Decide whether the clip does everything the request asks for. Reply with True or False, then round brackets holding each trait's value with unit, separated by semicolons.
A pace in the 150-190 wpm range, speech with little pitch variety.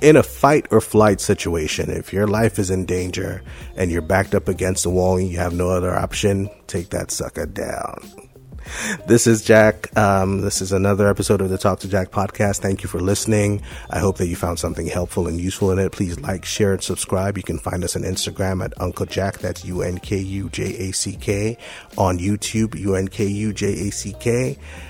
True (185 wpm; 2.2 semitones)